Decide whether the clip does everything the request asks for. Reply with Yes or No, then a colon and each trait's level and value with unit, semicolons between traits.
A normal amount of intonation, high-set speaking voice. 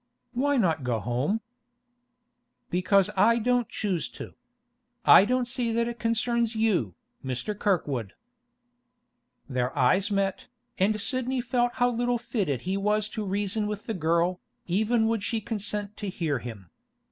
Yes: average, 5.0 semitones; high, 210 Hz